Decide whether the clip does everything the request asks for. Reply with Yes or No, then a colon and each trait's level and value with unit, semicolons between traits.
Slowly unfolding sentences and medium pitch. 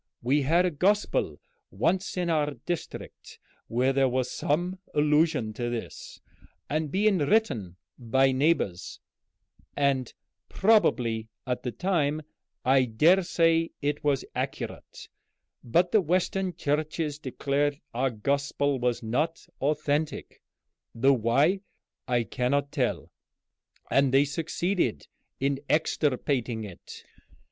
Yes: slow, 115 wpm; medium, 145 Hz